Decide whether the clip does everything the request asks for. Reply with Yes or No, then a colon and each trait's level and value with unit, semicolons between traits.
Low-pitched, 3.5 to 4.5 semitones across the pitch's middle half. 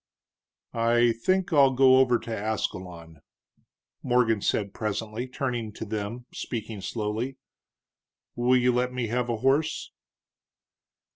No: low, 120 Hz; average, 2.8 semitones